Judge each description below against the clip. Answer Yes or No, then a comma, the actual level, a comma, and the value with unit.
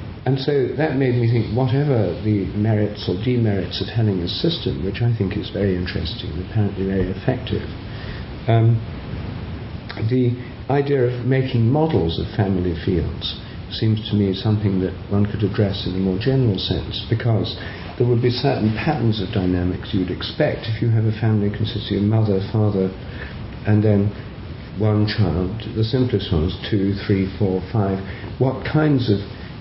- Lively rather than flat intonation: No, average, 3.5 semitones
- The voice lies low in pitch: Yes, low, 105 Hz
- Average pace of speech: Yes, average, 160 wpm